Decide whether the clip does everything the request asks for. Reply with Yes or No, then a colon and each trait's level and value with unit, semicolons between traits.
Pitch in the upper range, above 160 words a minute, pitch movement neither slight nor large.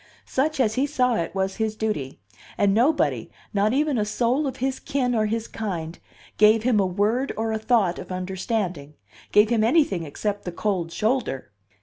Yes: high, 215 Hz; average, 185 wpm; average, 4.6 semitones